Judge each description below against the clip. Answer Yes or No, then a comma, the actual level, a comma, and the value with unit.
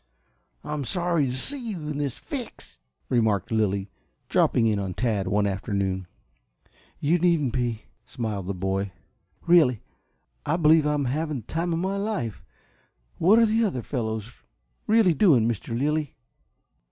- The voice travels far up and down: Yes, wide, 7.5 semitones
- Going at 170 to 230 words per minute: No, average, 145 wpm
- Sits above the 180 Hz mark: No, low, 130 Hz